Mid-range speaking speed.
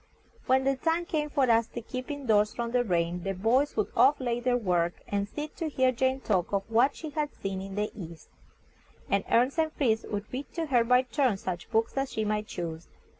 No: fast, 230 wpm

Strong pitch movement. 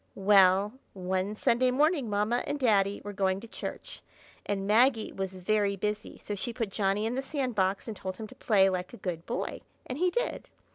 No: average, 3.9 semitones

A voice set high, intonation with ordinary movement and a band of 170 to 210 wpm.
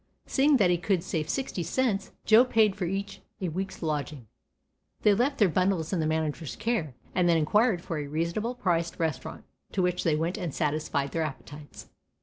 No: medium, 175 Hz; average, 4.4 semitones; average, 185 wpm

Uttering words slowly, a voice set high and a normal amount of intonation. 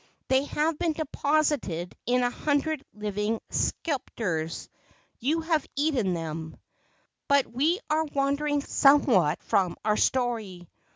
No: slow, 115 wpm; very high, 265 Hz; wide, 6.8 semitones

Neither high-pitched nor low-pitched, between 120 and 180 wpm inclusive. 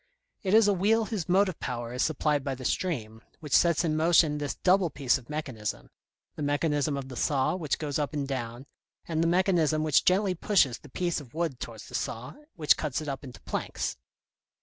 No: medium, 150 Hz; fast, 205 wpm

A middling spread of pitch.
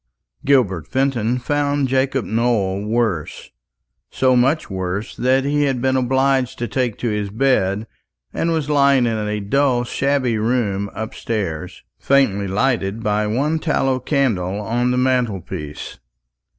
Yes: average, 4.3 semitones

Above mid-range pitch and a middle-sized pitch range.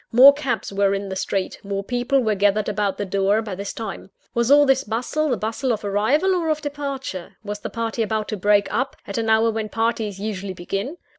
Yes: high, 220 Hz; average, 4.2 semitones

